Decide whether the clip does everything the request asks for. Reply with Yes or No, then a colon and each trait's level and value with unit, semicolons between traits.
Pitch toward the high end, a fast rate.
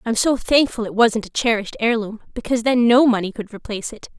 Yes: high, 225 Hz; fast, 215 wpm